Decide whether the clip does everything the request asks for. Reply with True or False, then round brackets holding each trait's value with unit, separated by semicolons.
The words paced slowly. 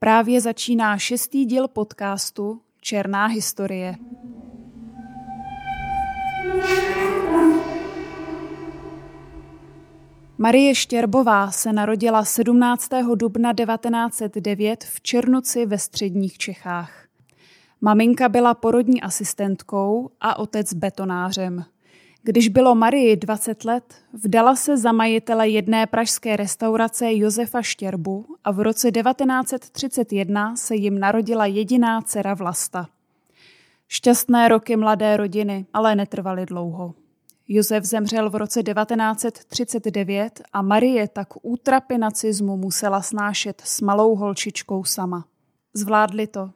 True (95 wpm)